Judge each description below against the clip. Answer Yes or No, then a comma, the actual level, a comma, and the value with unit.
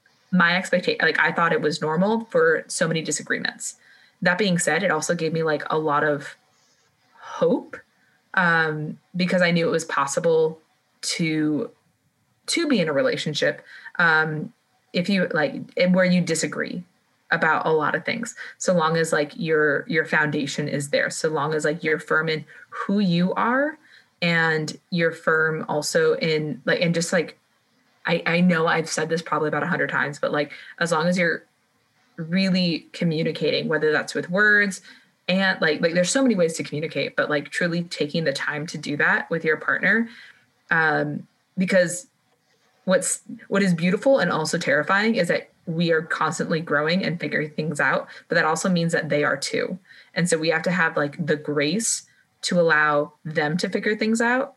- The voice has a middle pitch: Yes, medium, 170 Hz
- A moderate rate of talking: Yes, average, 180 wpm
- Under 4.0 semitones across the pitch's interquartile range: Yes, average, 3.5 semitones